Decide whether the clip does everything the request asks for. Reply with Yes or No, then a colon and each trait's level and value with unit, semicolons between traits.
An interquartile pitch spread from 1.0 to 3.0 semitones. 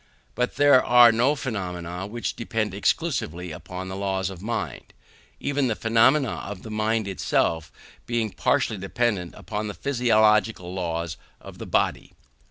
No: average, 4.2 semitones